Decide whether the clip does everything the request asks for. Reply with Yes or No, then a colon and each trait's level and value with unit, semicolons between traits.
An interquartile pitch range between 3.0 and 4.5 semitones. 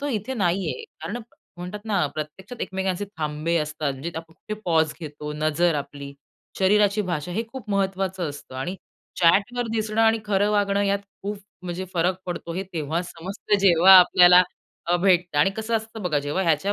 Yes: average, 4.0 semitones